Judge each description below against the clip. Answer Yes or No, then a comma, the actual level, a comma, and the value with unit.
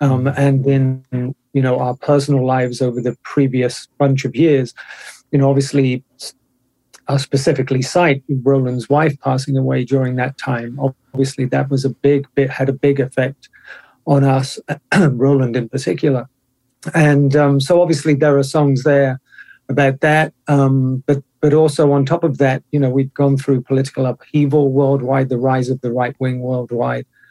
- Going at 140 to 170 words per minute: Yes, average, 165 wpm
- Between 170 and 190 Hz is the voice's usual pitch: No, low, 135 Hz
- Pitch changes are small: Yes, narrow, 1.6 semitones